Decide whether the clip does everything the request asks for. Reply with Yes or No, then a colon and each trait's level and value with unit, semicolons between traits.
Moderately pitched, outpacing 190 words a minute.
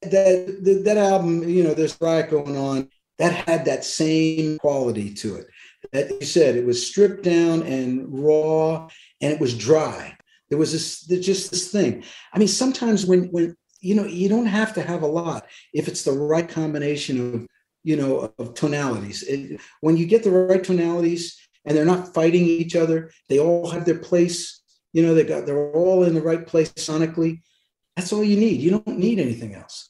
Yes: medium, 165 Hz; average, 200 wpm